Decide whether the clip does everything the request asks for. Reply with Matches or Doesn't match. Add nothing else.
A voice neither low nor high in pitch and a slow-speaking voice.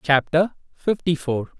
Matches